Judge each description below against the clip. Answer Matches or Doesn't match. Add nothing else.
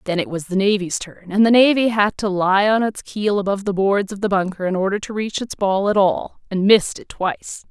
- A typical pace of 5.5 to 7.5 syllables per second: Matches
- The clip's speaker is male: Doesn't match